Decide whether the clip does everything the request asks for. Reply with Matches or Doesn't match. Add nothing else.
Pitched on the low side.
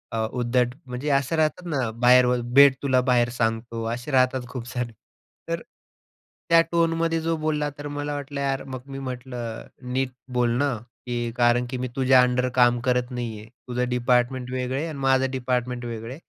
Matches